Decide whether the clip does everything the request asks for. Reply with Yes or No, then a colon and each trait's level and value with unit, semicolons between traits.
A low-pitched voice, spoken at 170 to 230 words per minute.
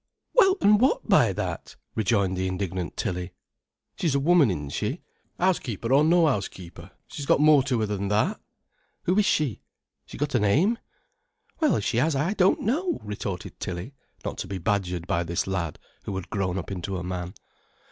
Yes: low, 105 Hz; average, 180 wpm